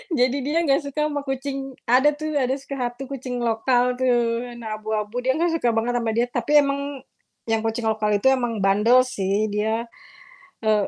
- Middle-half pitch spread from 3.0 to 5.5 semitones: Yes, average, 3.4 semitones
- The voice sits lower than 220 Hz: No, high, 245 Hz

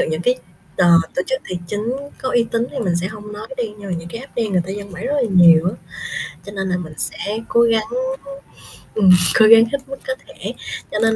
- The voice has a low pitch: No, high, 210 Hz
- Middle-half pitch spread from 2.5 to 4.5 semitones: Yes, average, 4.2 semitones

